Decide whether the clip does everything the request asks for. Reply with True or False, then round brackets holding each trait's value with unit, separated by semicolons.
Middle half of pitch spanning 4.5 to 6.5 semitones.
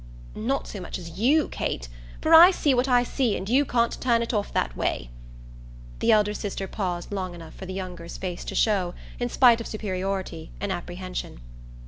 True (5.0 semitones)